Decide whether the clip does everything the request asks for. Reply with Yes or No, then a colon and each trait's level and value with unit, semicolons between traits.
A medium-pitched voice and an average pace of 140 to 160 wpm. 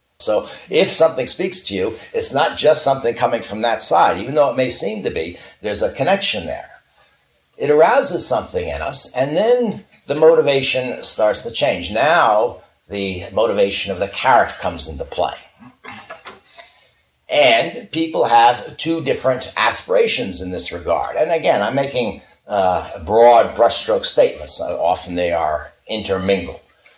Yes: medium, 155 Hz; average, 150 wpm